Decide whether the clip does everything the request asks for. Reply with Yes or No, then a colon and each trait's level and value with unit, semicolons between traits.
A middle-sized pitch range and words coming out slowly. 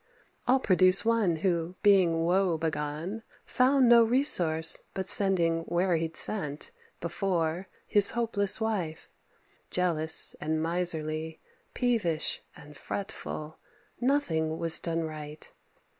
Yes: average, 4.1 semitones; slow, 110 wpm